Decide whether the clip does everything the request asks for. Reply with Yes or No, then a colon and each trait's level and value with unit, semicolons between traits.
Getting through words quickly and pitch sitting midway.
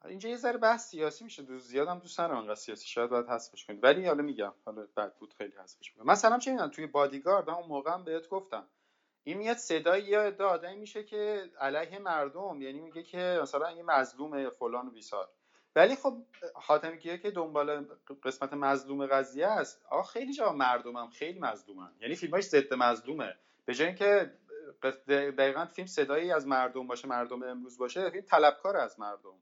Yes: fast, 175 wpm; medium, 155 Hz